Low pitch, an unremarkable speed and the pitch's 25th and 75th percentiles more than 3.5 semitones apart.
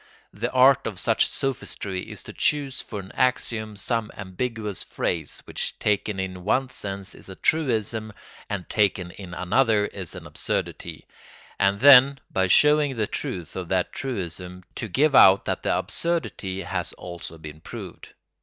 Yes: low, 105 Hz; average, 155 wpm; average, 5.3 semitones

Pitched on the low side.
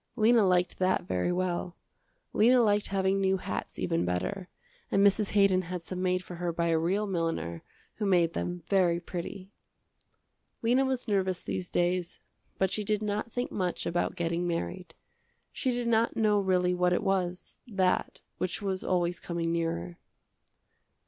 No: medium, 185 Hz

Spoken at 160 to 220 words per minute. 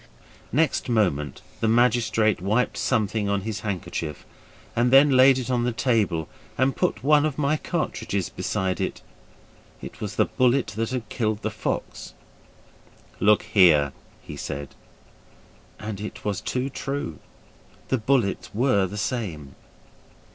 No: average, 140 wpm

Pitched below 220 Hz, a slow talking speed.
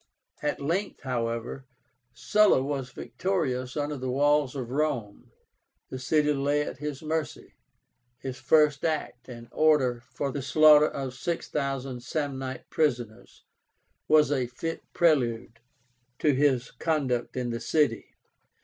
Yes: medium, 140 Hz; slow, 125 wpm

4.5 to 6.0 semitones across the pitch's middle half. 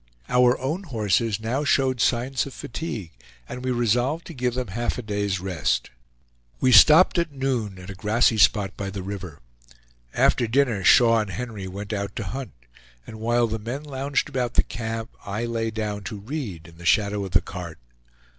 No: average, 4.0 semitones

